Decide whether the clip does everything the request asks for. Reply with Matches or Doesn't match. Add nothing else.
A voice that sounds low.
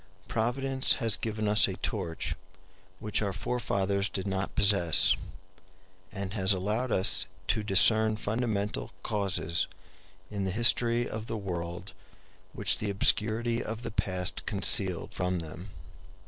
Matches